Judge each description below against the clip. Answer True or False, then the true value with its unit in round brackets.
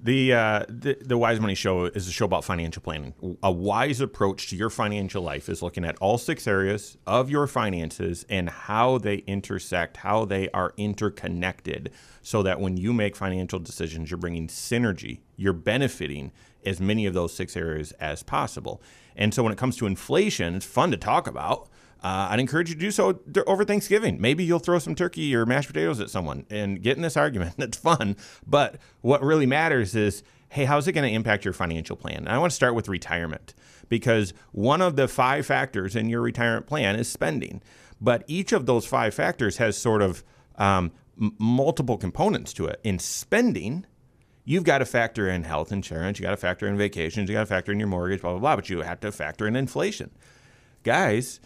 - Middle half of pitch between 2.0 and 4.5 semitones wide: False (5.4 semitones)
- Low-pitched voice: True (105 Hz)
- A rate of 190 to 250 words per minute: True (205 wpm)